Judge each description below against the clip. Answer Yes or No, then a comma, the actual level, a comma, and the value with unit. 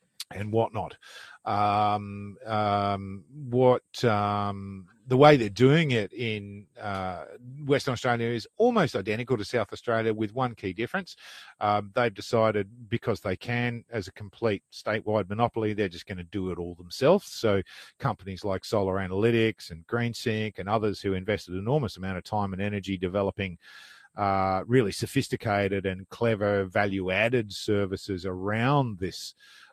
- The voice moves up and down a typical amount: Yes, average, 3.2 semitones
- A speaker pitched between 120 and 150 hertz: No, low, 105 Hz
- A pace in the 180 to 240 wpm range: No, average, 145 wpm